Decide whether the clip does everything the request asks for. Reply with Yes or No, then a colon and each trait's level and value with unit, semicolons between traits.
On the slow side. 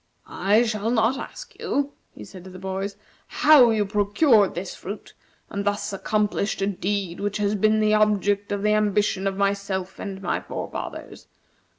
No: average, 170 wpm